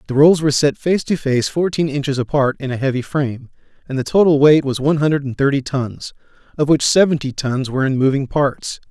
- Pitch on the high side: No, medium, 140 Hz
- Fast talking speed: Yes, fast, 215 wpm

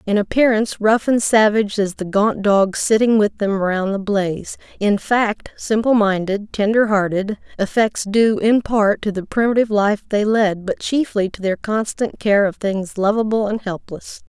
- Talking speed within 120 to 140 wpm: No, average, 175 wpm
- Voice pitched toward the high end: Yes, high, 210 Hz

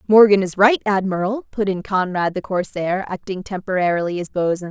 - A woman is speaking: Yes, female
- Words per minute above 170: No, average, 165 wpm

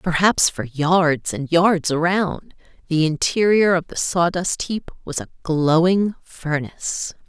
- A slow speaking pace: Yes, slow, 130 wpm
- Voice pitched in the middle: Yes, medium, 170 Hz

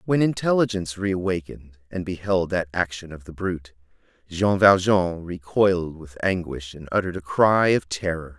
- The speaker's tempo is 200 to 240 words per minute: No, average, 155 wpm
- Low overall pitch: Yes, very low, 90 Hz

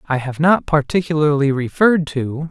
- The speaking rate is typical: Yes, average, 145 wpm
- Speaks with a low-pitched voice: No, medium, 150 Hz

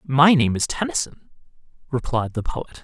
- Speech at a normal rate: Yes, average, 150 wpm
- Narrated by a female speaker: No, male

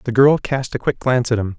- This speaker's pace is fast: Yes, fast, 300 wpm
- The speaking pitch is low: Yes, low, 125 Hz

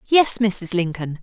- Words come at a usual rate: Yes, average, 145 wpm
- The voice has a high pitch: Yes, high, 200 Hz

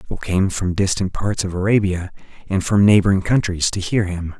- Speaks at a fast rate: No, average, 190 wpm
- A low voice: Yes, very low, 95 Hz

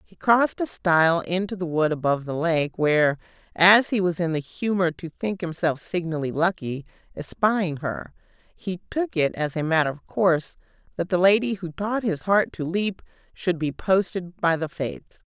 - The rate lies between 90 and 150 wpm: No, average, 185 wpm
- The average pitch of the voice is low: No, medium, 175 Hz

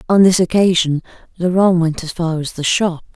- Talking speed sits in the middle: Yes, average, 190 wpm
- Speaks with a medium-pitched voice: Yes, medium, 175 Hz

